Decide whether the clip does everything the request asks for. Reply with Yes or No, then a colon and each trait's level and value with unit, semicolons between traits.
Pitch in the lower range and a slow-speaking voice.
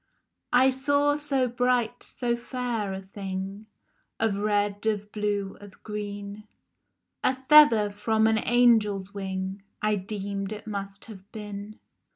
No: high, 210 Hz; slow, 130 wpm